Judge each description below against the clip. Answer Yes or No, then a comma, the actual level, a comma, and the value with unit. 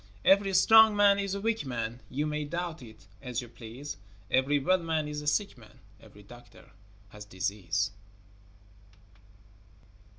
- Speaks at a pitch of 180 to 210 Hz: No, medium, 145 Hz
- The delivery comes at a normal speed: Yes, average, 145 wpm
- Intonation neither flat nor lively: No, wide, 8.2 semitones